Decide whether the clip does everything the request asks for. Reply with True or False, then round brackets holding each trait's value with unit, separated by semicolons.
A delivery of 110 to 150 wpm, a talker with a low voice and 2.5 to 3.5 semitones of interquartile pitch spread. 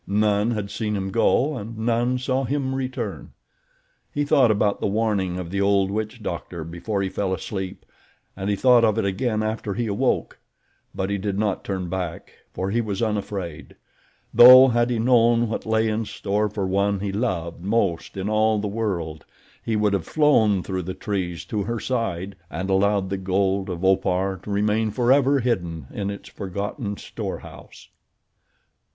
False (175 wpm; 105 Hz; 3.0 semitones)